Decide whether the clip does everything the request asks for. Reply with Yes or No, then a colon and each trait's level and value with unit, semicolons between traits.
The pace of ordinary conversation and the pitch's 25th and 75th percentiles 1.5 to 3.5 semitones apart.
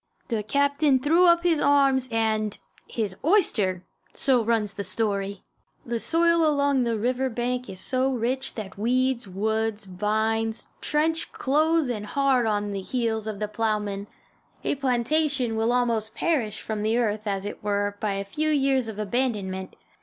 No: average, 160 wpm; average, 4.4 semitones